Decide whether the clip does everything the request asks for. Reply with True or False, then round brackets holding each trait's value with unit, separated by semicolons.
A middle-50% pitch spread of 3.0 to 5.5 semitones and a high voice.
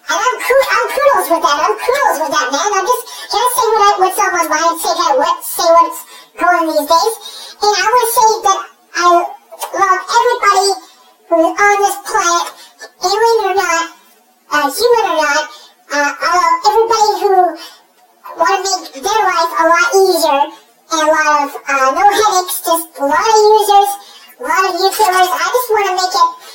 True (4.3 semitones; 380 Hz)